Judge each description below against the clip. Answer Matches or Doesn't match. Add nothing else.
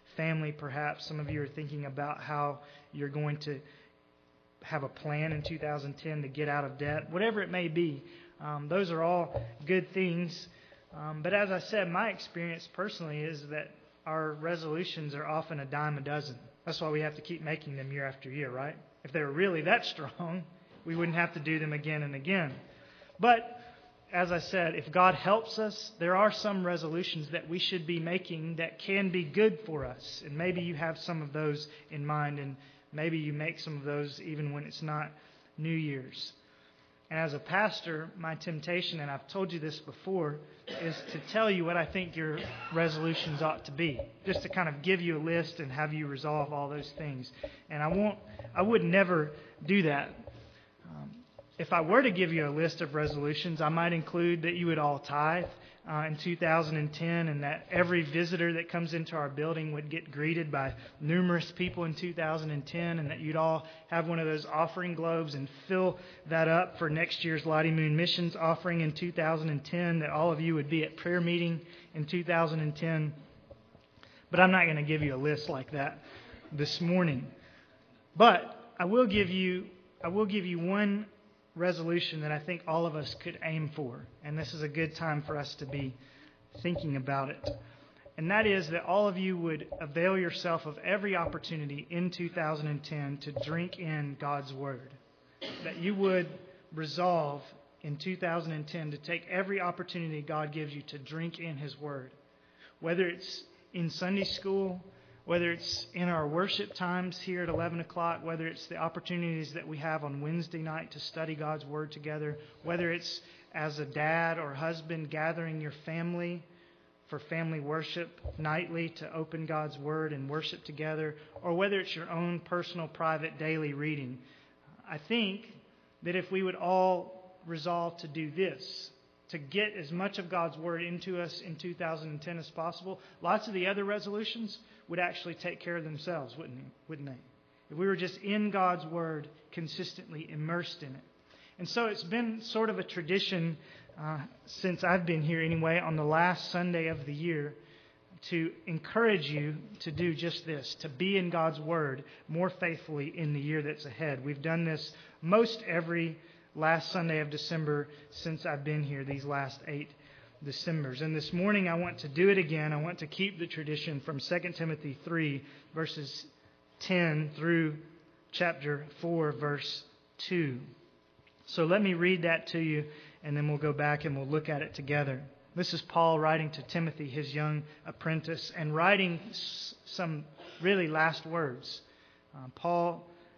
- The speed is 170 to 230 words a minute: Matches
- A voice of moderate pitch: Matches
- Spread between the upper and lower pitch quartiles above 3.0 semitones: Doesn't match